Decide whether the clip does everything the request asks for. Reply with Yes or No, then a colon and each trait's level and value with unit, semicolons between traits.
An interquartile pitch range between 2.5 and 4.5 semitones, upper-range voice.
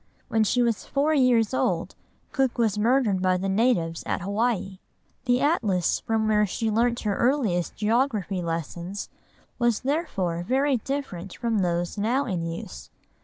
No: average, 5.2 semitones; high, 220 Hz